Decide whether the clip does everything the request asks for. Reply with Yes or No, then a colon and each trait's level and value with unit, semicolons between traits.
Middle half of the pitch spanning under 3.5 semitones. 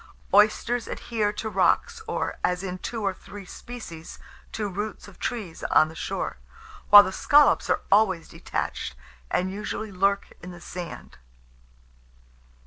Yes: average, 3.1 semitones